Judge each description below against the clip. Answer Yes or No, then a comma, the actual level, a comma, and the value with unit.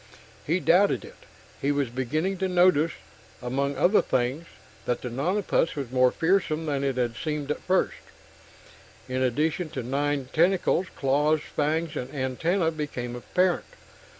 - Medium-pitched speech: Yes, medium, 150 Hz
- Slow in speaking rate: No, average, 145 wpm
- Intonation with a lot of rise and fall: No, average, 4.4 semitones